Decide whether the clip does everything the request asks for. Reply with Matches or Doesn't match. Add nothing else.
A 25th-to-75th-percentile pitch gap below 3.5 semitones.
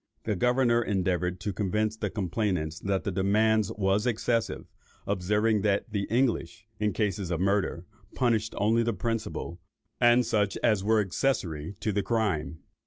Matches